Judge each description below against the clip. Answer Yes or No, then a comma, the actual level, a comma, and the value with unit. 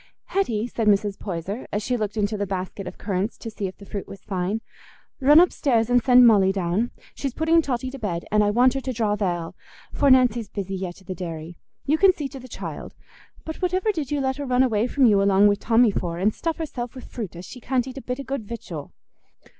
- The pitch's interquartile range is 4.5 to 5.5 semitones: Yes, average, 4.8 semitones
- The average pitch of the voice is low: No, high, 225 Hz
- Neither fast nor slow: No, fast, 240 wpm